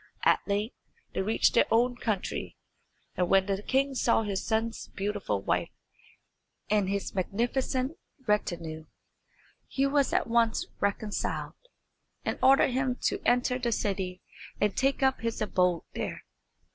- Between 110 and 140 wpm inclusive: Yes, slow, 135 wpm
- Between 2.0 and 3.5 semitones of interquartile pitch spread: No, average, 4.2 semitones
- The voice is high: Yes, high, 220 Hz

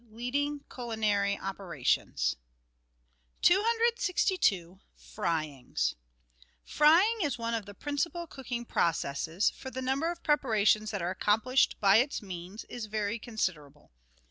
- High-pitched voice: Yes, high, 220 Hz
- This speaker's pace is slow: Yes, slow, 115 wpm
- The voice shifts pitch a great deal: Yes, wide, 6.9 semitones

